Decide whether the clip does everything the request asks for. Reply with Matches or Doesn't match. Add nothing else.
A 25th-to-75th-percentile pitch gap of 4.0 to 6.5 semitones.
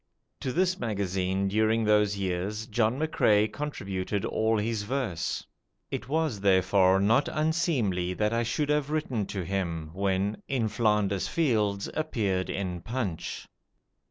Matches